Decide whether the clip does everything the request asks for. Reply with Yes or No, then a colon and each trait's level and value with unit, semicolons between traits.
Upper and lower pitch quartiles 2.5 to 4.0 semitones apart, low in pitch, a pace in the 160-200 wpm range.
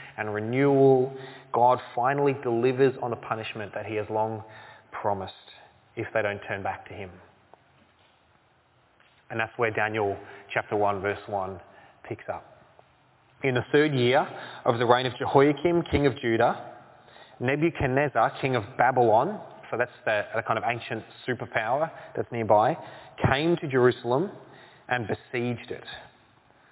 No: average, 3.6 semitones; low, 120 Hz; slow, 135 wpm